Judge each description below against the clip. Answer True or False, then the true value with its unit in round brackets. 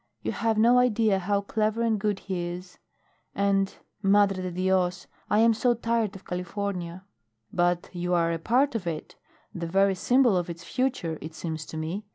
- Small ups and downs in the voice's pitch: False (3.7 semitones)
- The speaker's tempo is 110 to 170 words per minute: False (185 wpm)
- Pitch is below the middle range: False (195 Hz)